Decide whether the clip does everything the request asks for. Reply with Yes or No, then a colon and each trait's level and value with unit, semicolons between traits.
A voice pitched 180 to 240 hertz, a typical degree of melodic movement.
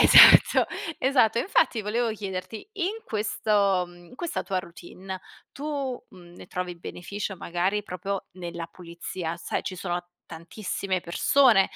Yes: high, 190 Hz; average, 4.0 semitones